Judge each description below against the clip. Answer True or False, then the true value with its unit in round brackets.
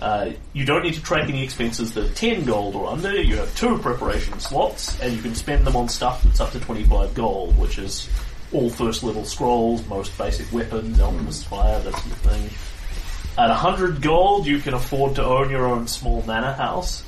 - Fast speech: True (210 wpm)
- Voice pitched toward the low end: True (120 Hz)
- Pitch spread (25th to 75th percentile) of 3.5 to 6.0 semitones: True (4.6 semitones)